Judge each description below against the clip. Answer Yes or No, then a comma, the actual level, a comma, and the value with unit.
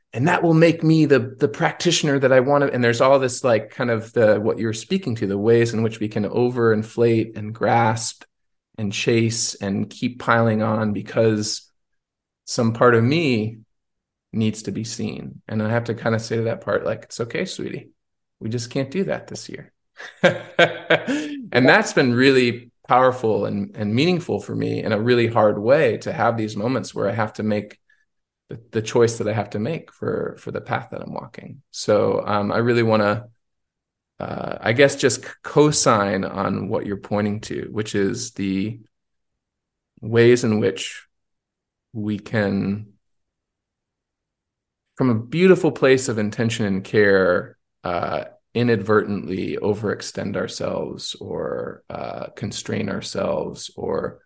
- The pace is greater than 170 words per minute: No, average, 165 wpm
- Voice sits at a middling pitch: No, low, 115 Hz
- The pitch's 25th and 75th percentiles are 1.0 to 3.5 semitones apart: Yes, average, 3.2 semitones